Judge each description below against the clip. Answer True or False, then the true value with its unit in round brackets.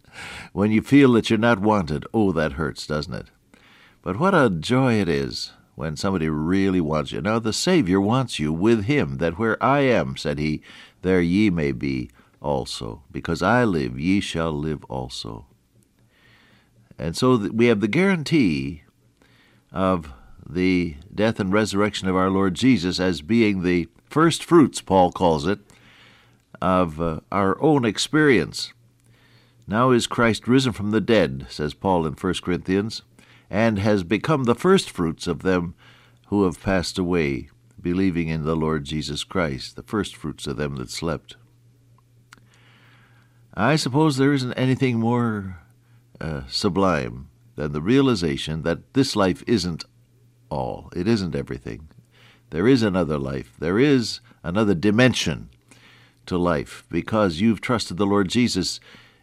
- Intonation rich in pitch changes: True (6.2 semitones)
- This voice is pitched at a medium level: False (100 Hz)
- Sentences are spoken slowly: False (145 wpm)